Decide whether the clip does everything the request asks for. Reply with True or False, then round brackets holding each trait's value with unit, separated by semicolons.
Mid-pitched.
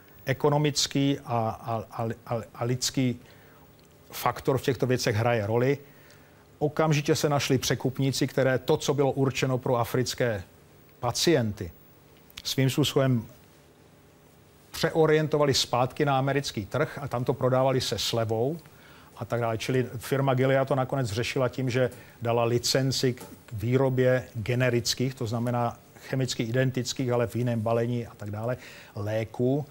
False (130 Hz)